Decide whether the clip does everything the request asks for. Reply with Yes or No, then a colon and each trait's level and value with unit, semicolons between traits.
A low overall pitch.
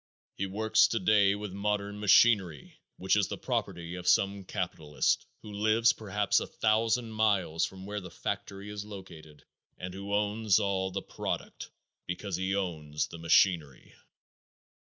Yes: low, 100 Hz